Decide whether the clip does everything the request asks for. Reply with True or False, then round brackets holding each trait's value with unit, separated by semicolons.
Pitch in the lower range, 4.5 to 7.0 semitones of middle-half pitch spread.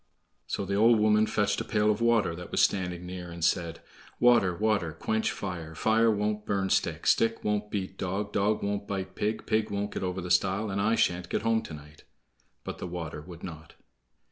False (100 Hz; 3.2 semitones)